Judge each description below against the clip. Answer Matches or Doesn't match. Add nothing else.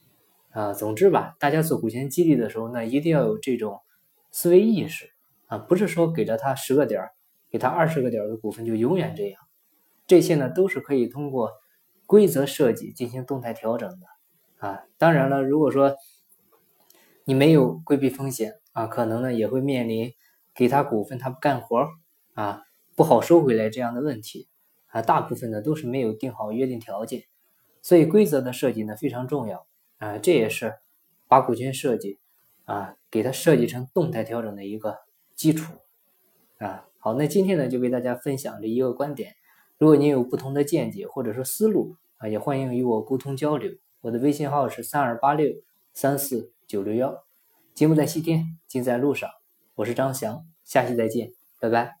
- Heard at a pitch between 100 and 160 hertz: Matches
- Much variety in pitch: Doesn't match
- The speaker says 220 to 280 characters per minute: Matches